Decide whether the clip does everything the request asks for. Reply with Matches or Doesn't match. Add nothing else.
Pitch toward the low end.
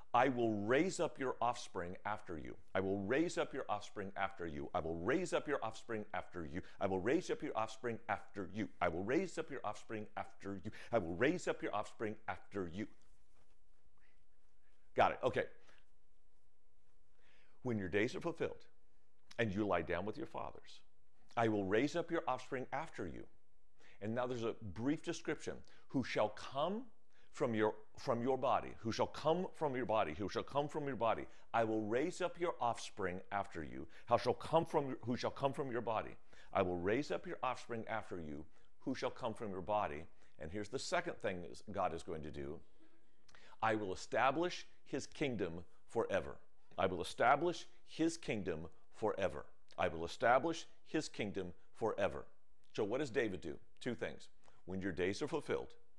Matches